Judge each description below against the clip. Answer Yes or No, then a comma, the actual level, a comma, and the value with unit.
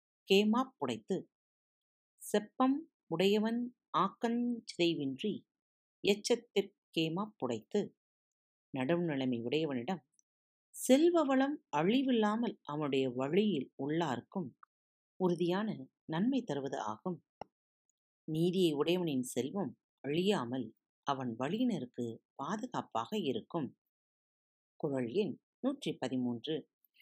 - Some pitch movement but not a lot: No, wide, 8.6 semitones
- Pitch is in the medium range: Yes, medium, 180 Hz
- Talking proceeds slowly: Yes, slow, 65 wpm